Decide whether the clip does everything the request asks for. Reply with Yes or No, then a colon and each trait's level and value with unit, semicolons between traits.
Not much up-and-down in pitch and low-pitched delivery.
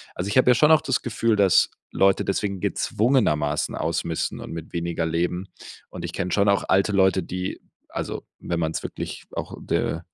No: average, 3.5 semitones; very low, 95 Hz